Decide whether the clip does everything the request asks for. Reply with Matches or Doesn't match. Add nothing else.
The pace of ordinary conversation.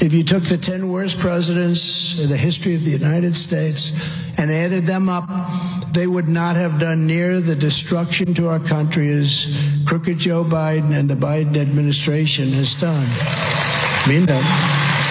Matches